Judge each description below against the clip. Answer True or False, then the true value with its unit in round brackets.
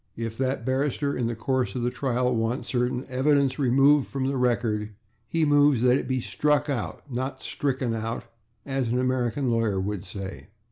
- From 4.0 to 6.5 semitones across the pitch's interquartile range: False (2.9 semitones)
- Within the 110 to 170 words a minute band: False (180 wpm)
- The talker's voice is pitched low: True (125 Hz)